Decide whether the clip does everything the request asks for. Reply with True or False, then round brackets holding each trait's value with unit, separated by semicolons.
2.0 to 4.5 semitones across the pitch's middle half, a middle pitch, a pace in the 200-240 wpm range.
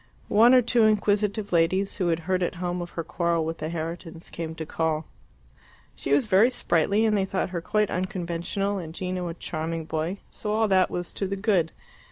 True (3.5 semitones; 180 Hz; 205 wpm)